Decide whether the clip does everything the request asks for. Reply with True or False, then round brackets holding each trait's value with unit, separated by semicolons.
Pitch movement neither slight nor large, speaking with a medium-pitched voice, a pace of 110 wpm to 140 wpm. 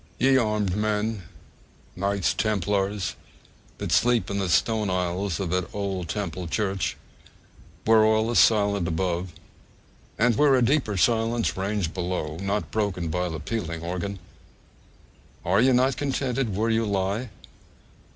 False (3.4 semitones; 100 Hz; 135 wpm)